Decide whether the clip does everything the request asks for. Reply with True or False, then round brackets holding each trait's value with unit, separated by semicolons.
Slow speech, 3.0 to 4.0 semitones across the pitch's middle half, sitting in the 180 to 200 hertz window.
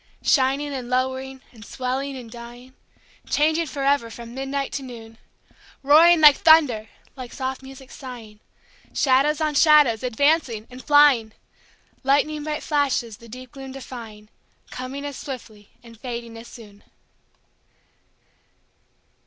False (125 wpm; 3.3 semitones; 260 Hz)